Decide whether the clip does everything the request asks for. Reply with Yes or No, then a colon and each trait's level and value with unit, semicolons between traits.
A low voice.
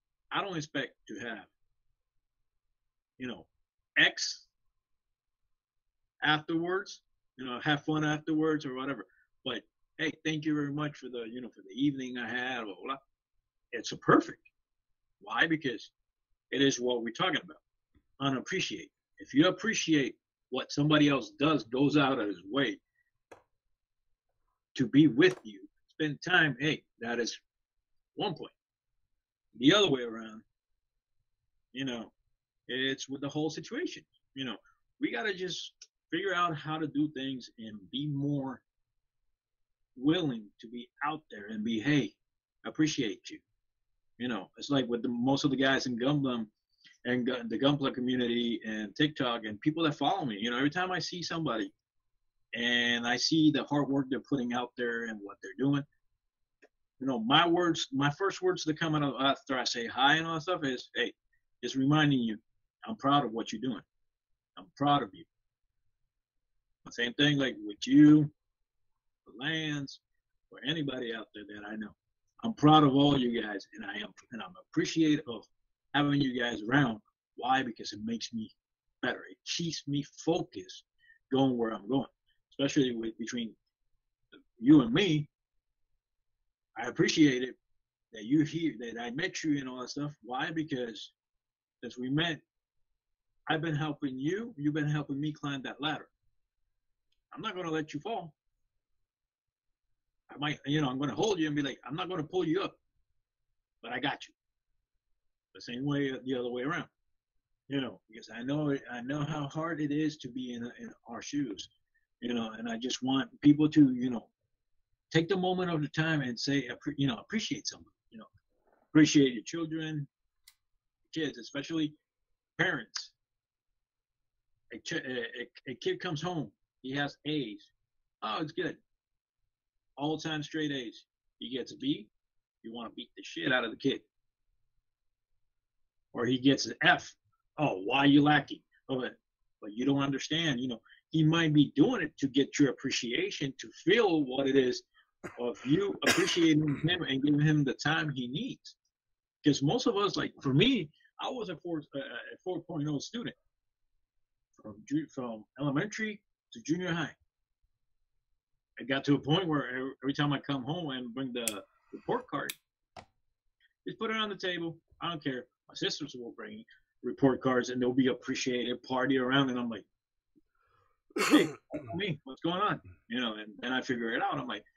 No: medium, 145 Hz